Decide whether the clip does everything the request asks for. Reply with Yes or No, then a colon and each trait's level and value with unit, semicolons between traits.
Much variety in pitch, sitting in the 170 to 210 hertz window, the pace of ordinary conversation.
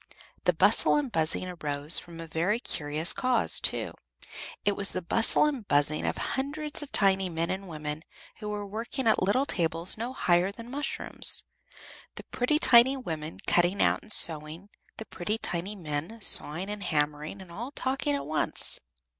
Yes: wide, 6.1 semitones; high, 190 Hz; average, 170 wpm